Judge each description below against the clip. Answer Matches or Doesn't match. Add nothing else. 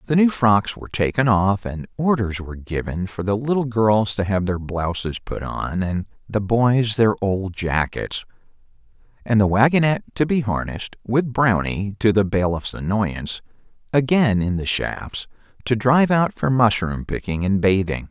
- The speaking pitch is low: Matches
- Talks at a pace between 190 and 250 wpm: Doesn't match